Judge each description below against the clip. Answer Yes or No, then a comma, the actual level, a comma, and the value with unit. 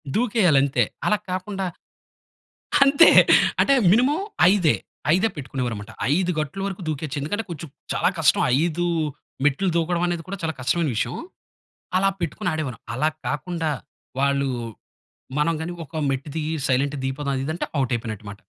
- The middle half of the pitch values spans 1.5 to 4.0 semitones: No, average, 4.8 semitones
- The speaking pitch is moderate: Yes, medium, 160 Hz